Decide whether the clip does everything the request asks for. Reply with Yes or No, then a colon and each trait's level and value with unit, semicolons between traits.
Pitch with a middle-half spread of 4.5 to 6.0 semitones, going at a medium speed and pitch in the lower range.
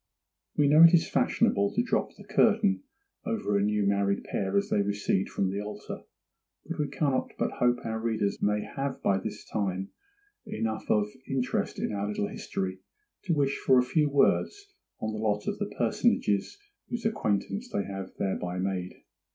Yes: wide, 5.5 semitones; average, 175 wpm; low, 105 Hz